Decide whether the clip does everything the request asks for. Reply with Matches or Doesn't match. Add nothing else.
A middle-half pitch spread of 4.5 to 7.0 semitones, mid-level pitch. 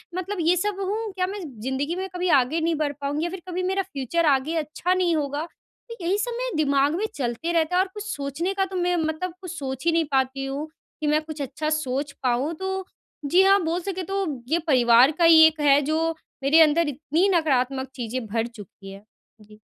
Doesn't match